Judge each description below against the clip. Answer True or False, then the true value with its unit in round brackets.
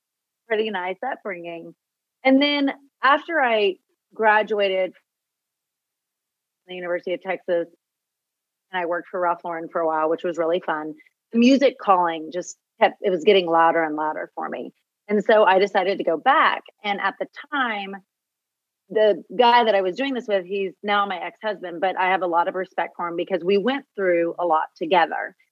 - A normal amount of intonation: True (3.6 semitones)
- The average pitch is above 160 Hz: True (190 Hz)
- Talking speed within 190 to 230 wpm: False (180 wpm)